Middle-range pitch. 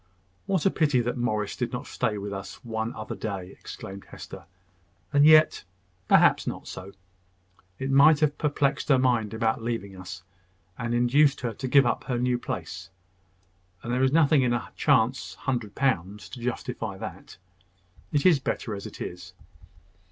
No: low, 120 Hz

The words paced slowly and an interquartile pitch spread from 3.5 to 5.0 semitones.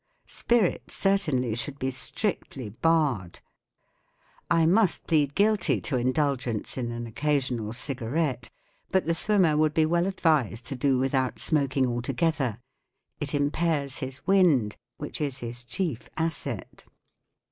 Yes: slow, 130 wpm; average, 4.7 semitones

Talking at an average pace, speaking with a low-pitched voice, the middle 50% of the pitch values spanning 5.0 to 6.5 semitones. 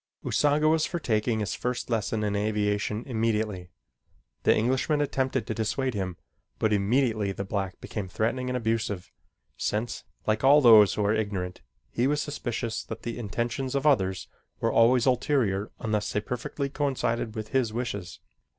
No: average, 160 wpm; low, 115 Hz; average, 3.6 semitones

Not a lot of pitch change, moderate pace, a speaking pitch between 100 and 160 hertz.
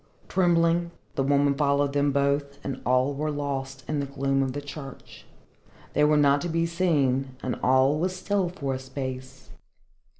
Yes: narrow, 2.1 semitones; average, 170 wpm; medium, 140 Hz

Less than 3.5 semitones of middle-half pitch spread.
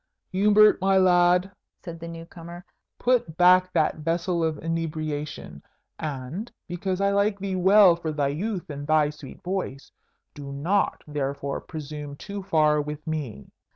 No: average, 3.9 semitones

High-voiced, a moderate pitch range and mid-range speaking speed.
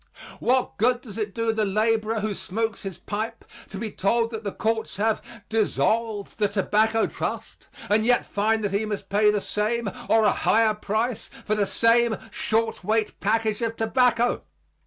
No: high, 220 Hz; narrow, 1.5 semitones; average, 175 wpm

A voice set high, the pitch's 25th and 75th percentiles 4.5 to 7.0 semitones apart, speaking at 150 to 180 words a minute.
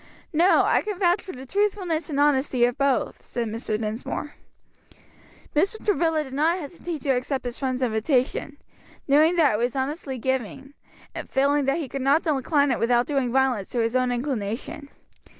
No: very high, 275 Hz; average, 3.7 semitones; average, 175 wpm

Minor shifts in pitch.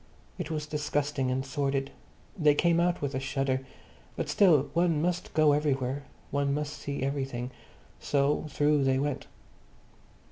Yes: narrow, 1.8 semitones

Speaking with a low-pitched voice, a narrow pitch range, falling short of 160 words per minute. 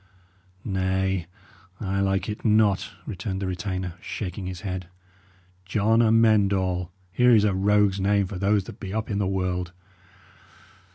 Yes: very low, 95 Hz; narrow, 1.9 semitones; average, 150 wpm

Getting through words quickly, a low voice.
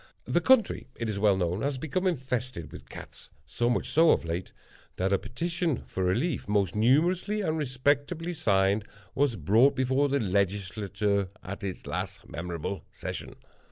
No: average, 155 wpm; low, 115 Hz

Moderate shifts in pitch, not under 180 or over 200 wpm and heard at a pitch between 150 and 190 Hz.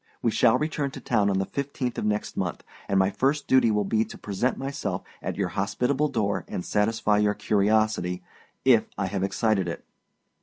No: average, 4.0 semitones; average, 190 wpm; low, 105 Hz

